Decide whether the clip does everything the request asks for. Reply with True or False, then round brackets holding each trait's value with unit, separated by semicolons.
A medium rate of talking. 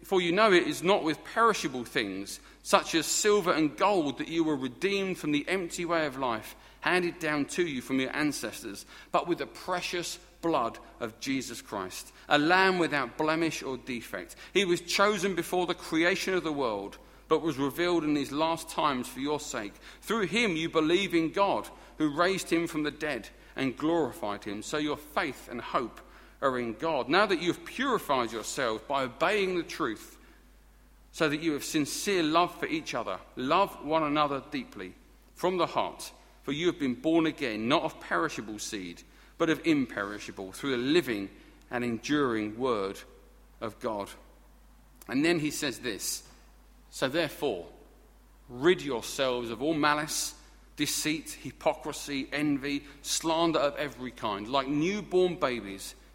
True (165 wpm)